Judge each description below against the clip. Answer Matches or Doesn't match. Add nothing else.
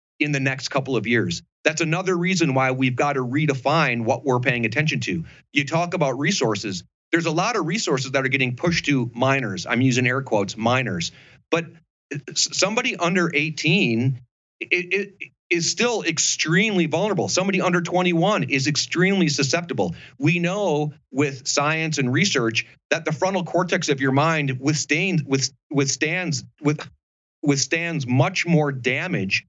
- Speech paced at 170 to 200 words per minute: Doesn't match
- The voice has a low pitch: Doesn't match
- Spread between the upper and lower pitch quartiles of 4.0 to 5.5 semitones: Matches